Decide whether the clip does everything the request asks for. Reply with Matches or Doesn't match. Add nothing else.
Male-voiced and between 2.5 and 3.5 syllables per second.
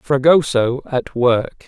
Matches